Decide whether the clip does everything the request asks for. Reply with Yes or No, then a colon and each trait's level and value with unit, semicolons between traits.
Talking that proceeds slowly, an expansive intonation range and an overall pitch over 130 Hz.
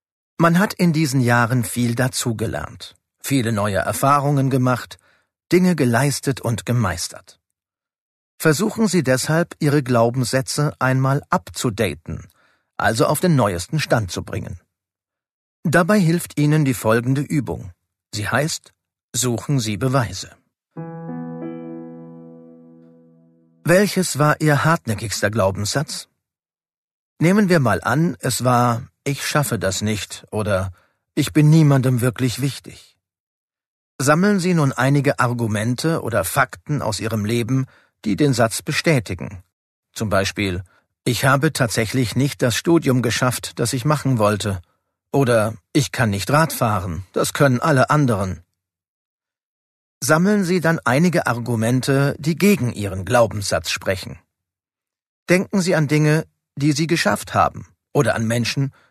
No: slow, 120 wpm; wide, 6.1 semitones; low, 125 Hz